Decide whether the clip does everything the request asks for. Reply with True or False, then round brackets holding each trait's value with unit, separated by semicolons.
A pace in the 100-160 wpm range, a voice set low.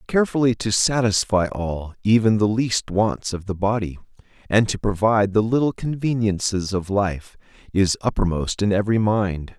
True (150 wpm; 105 Hz)